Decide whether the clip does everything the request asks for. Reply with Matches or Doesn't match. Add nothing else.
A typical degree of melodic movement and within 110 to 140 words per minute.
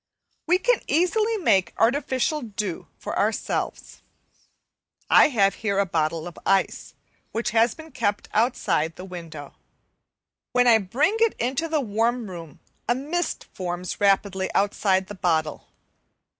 Doesn't match